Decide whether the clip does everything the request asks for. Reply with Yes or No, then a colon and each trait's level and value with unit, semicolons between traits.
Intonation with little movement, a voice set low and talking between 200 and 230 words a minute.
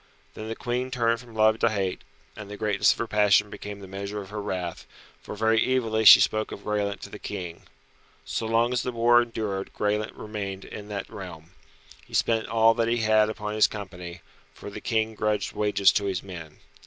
Yes: narrow, 2.1 semitones; low, 105 Hz; fast, 205 wpm